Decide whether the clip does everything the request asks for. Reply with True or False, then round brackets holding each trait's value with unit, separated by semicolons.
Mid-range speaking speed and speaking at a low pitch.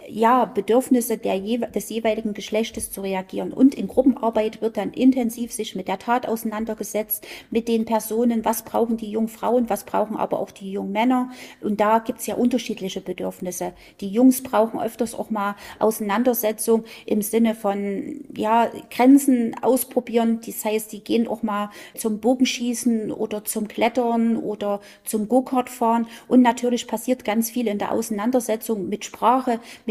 False (160 wpm; 225 Hz)